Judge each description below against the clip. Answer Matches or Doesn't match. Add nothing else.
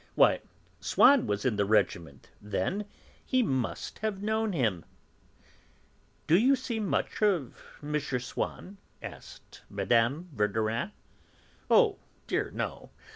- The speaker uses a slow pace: Matches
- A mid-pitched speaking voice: Matches